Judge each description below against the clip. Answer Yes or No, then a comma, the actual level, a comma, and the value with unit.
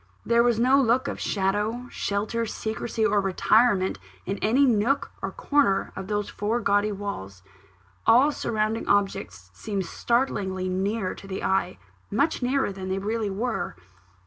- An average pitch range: Yes, average, 3.4 semitones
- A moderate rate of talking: Yes, average, 150 wpm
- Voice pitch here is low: No, high, 210 Hz